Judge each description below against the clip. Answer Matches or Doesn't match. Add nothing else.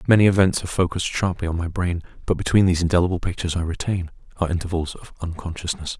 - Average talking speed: Matches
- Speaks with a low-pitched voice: Matches